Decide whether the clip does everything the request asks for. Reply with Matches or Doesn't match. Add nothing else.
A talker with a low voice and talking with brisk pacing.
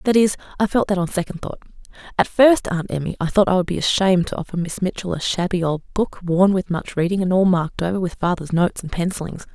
Doesn't match